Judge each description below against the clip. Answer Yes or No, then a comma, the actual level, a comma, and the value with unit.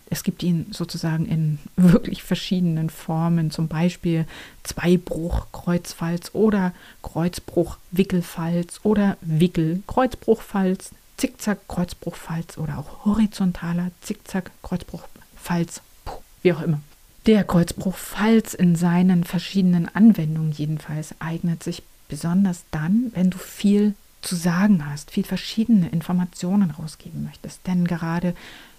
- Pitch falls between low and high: Yes, medium, 175 Hz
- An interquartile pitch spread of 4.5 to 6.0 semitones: No, average, 2.8 semitones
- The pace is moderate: No, slow, 100 wpm